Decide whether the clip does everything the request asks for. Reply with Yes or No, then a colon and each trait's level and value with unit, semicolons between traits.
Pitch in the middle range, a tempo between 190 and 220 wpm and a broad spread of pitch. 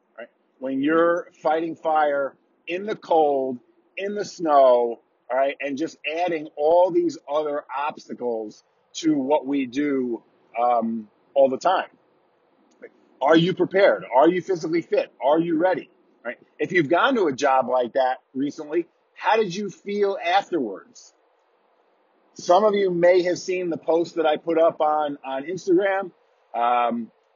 No: medium, 160 Hz; average, 150 wpm; wide, 5.9 semitones